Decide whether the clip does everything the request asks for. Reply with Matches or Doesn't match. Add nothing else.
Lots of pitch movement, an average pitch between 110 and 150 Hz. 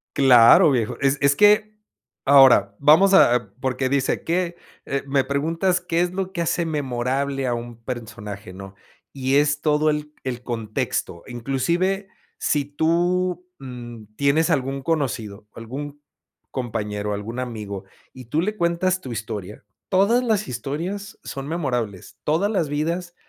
Matches